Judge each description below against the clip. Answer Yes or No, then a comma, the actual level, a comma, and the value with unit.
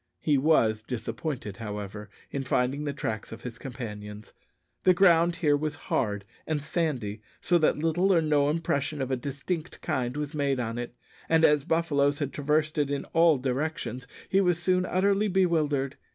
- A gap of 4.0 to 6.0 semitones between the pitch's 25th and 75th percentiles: Yes, average, 4.6 semitones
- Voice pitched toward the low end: No, medium, 145 Hz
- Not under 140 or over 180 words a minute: Yes, average, 170 wpm